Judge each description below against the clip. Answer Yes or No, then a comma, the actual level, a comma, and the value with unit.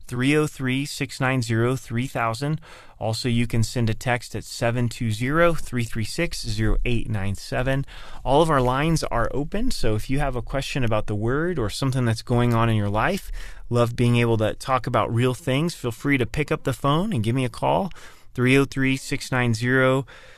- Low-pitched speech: Yes, low, 125 Hz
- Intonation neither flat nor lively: Yes, average, 3.1 semitones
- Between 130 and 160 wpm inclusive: Yes, average, 155 wpm